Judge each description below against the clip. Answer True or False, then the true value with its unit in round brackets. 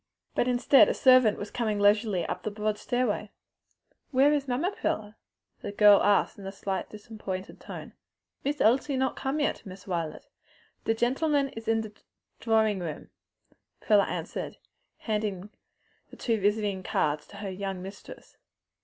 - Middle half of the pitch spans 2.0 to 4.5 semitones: True (3.8 semitones)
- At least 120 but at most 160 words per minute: True (155 wpm)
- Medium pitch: False (215 Hz)